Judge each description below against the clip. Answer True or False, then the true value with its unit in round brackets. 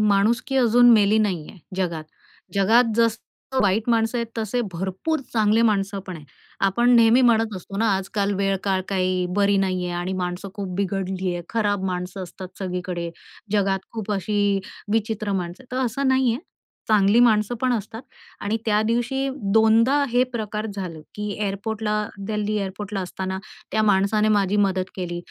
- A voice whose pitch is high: True (205 Hz)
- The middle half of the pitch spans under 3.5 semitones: True (2.9 semitones)